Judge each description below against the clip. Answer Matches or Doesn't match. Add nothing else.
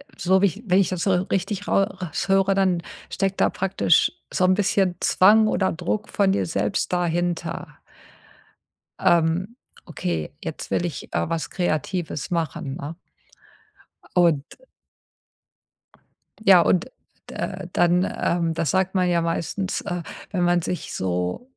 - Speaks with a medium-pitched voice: Matches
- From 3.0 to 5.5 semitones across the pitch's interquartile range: Doesn't match